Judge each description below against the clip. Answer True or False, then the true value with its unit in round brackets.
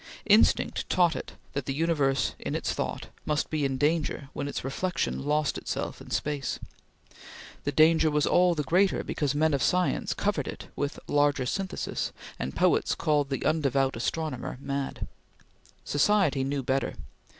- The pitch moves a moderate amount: True (3.0 semitones)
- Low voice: False (145 Hz)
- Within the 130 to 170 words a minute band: True (155 wpm)